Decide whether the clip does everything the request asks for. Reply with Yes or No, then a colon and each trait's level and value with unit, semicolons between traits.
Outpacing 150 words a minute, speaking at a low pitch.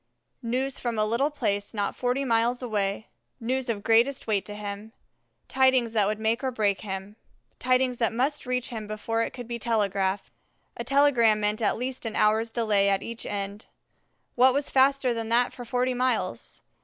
No: average, 180 wpm; high, 230 Hz